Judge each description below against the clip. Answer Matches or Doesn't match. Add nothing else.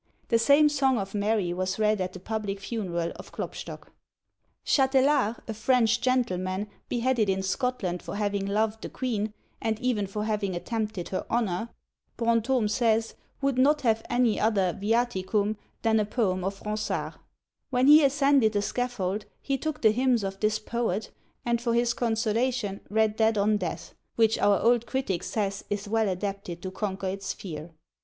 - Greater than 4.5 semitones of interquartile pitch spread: Doesn't match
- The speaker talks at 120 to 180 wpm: Matches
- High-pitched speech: Matches